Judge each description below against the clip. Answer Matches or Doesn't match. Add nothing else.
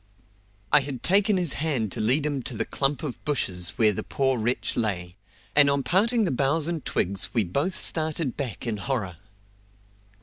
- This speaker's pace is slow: Doesn't match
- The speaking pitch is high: Doesn't match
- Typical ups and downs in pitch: Doesn't match